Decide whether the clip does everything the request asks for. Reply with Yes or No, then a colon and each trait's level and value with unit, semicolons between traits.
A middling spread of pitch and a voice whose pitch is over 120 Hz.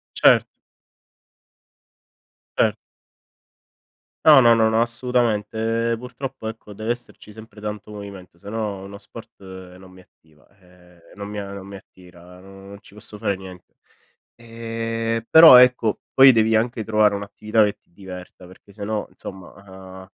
No: average, 3.0 semitones; low, 105 Hz